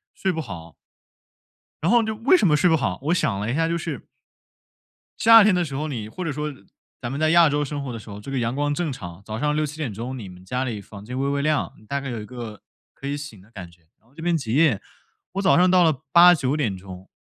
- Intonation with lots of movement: Yes, wide, 6.3 semitones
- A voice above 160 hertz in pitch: No, medium, 140 Hz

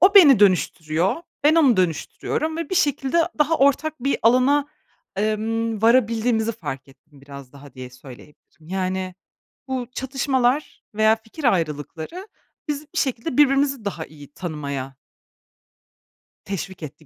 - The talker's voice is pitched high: Yes, high, 220 Hz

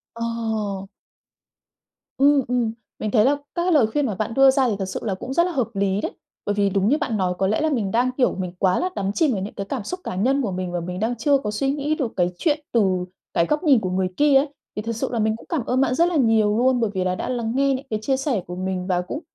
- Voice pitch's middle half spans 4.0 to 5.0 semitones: No, wide, 5.6 semitones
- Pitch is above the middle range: Yes, high, 225 Hz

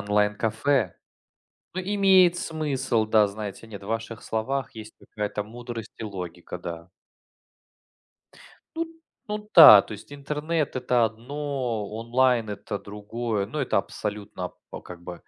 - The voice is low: Yes, low, 115 Hz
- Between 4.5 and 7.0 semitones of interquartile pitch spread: Yes, average, 5.2 semitones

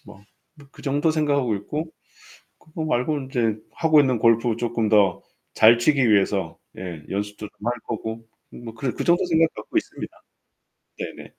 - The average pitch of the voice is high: No, low, 120 Hz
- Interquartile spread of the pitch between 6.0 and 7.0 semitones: No, wide, 5.6 semitones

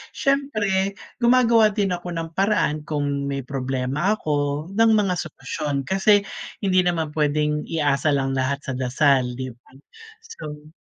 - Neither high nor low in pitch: Yes, medium, 155 Hz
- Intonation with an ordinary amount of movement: No, wide, 5.8 semitones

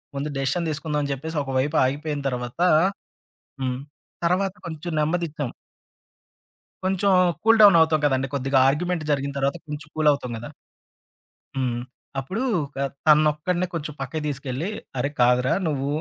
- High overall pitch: No, medium, 150 Hz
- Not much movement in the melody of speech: No, average, 3.2 semitones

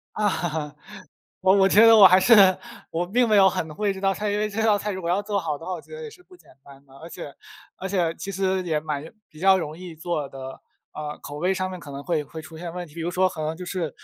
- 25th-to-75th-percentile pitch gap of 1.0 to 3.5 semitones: No, average, 3.9 semitones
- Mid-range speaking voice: Yes, medium, 180 Hz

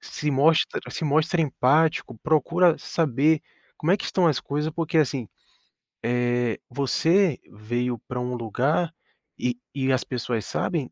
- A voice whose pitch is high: No, medium, 140 Hz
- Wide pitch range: No, average, 4.5 semitones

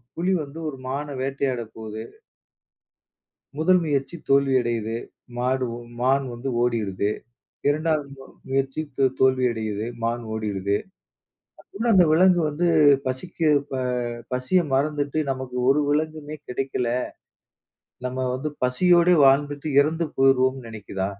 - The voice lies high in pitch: No, low, 135 Hz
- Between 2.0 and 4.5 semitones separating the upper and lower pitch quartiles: Yes, average, 3.8 semitones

